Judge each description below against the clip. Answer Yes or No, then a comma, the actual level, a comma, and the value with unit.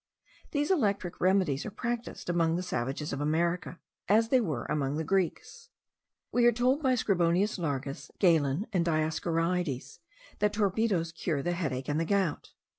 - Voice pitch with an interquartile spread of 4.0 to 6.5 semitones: Yes, average, 5.3 semitones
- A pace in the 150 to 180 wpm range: Yes, average, 155 wpm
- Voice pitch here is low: No, medium, 175 Hz